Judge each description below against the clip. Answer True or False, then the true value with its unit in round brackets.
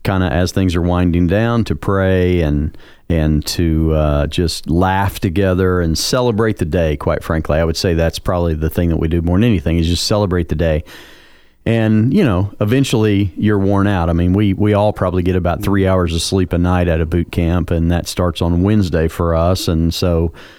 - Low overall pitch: True (90 Hz)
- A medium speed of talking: False (215 wpm)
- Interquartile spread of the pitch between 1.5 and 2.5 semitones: False (2.9 semitones)